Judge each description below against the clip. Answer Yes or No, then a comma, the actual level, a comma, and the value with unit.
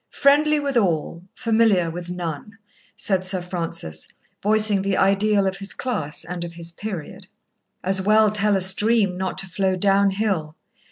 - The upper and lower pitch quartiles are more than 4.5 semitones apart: No, average, 3.2 semitones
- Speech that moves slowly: No, average, 155 wpm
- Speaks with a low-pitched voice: No, high, 195 Hz